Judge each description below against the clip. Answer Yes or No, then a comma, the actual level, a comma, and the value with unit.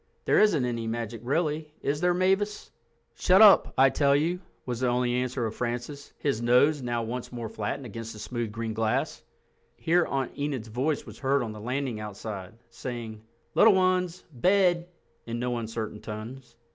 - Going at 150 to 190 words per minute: Yes, average, 170 wpm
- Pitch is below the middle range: Yes, low, 125 Hz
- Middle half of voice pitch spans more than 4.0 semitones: Yes, average, 4.7 semitones